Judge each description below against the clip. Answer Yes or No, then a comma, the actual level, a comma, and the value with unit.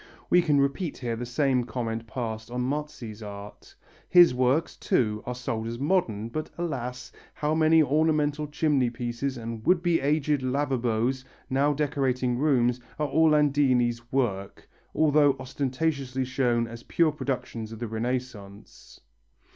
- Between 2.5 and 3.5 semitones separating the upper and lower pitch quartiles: No, average, 4.0 semitones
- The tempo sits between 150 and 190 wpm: No, slow, 135 wpm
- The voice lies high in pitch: No, low, 130 Hz